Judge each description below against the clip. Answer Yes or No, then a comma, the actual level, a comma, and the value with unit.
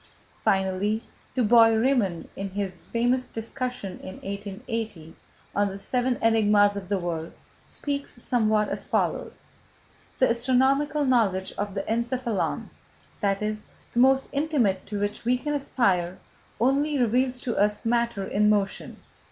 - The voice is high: Yes, high, 220 Hz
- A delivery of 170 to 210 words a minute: No, slow, 135 wpm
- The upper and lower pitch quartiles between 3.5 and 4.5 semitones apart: Yes, average, 4.0 semitones